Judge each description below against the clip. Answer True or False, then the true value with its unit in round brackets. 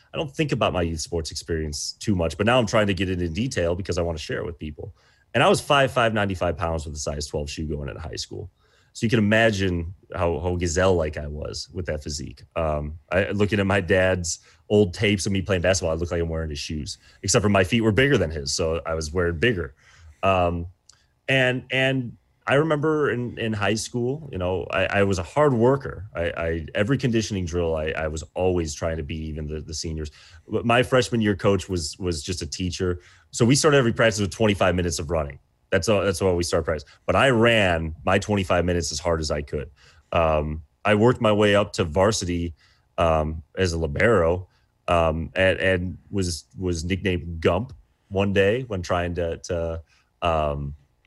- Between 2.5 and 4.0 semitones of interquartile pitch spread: False (4.4 semitones)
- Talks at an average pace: False (215 wpm)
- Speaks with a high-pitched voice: False (90 Hz)